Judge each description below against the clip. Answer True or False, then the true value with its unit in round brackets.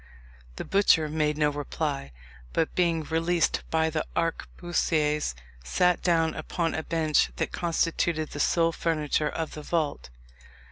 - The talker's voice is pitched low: False (160 Hz)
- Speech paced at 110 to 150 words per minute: True (135 wpm)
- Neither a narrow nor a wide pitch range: False (1.7 semitones)